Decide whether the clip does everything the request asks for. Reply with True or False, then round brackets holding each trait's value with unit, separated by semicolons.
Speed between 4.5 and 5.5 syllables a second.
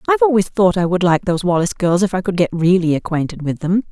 False (6.9 syllables/s)